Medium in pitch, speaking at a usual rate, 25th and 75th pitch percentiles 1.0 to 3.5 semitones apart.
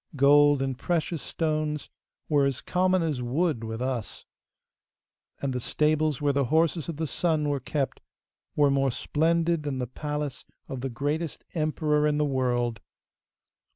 Yes: medium, 145 Hz; average, 155 wpm; average, 2.8 semitones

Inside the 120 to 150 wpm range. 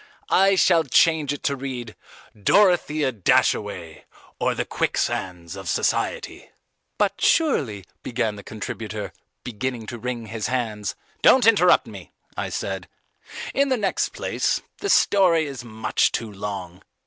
Yes: slow, 135 wpm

